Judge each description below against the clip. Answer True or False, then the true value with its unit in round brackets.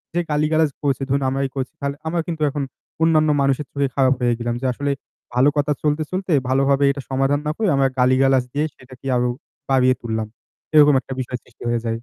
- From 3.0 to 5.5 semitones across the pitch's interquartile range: False (2.5 semitones)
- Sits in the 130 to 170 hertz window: True (135 Hz)